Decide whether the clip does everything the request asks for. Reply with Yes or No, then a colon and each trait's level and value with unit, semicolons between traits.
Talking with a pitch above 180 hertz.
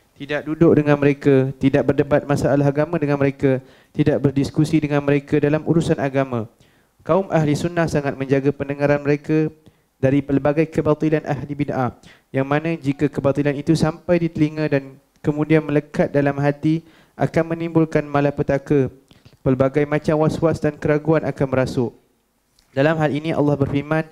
No: medium, 145 Hz